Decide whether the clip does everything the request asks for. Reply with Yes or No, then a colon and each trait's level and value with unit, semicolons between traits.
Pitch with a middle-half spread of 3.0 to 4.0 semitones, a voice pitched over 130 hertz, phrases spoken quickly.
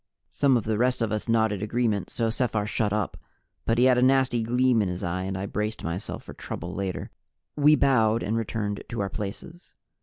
No: average, 3.3 semitones; low, 110 Hz; fast, 210 wpm